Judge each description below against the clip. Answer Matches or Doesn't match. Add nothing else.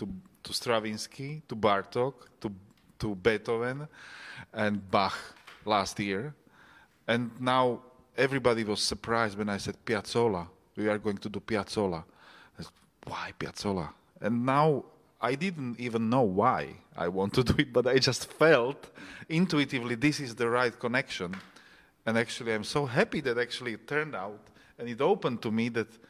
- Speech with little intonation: Doesn't match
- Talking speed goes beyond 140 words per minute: Matches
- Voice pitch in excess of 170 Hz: Doesn't match